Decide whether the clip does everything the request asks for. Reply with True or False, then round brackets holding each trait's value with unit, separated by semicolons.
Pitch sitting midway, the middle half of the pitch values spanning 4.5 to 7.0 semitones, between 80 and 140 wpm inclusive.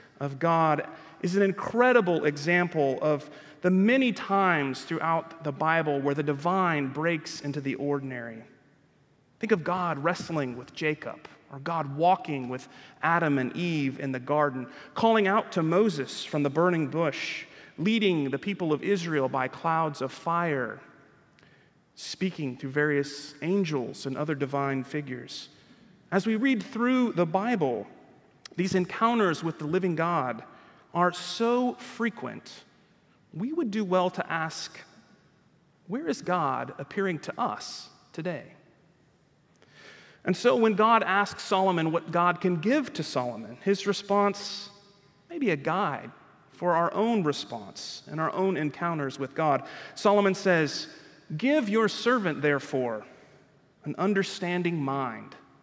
True (165 Hz; 5.2 semitones; 135 wpm)